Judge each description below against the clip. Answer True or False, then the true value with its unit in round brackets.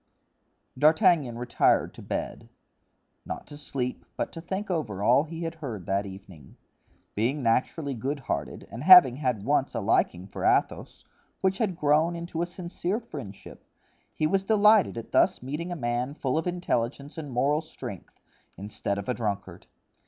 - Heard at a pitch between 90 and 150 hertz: True (140 Hz)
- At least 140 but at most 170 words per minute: True (155 wpm)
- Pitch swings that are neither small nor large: False (6.5 semitones)